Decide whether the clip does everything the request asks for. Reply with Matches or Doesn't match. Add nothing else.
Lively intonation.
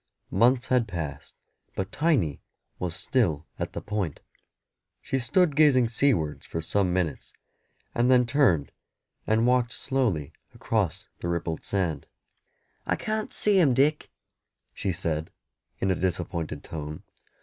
Matches